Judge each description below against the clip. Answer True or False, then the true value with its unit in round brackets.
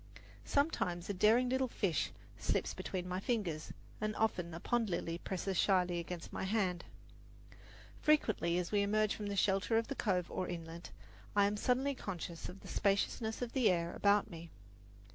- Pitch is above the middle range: True (195 Hz)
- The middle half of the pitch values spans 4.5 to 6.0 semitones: False (3.9 semitones)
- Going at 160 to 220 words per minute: True (170 wpm)